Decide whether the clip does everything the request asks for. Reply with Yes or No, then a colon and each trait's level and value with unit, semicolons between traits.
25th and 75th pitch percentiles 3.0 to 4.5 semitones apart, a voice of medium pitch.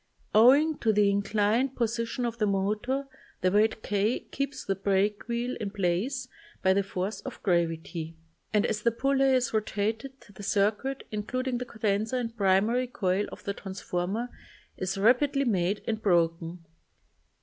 No: average, 3.9 semitones; high, 215 Hz